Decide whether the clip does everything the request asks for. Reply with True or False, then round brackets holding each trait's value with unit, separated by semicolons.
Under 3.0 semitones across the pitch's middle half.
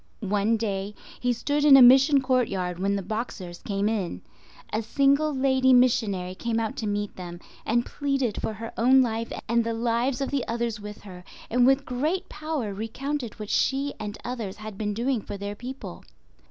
False (4.2 semitones)